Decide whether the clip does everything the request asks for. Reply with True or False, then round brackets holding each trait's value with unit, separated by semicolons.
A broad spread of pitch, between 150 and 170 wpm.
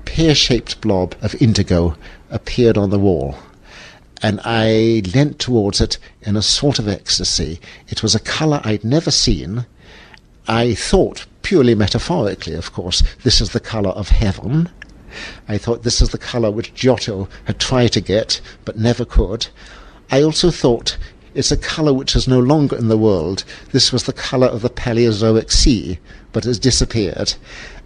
False (3.7 semitones; 165 wpm)